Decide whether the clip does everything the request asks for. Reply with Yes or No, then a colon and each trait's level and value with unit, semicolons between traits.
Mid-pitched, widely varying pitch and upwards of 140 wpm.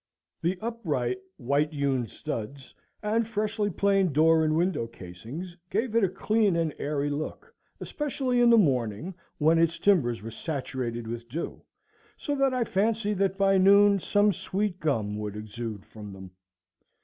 Yes: medium, 165 Hz; wide, 8.9 semitones; average, 155 wpm